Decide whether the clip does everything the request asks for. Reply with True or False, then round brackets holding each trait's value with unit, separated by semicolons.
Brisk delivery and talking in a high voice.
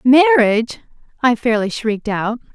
False (120 wpm; 240 Hz)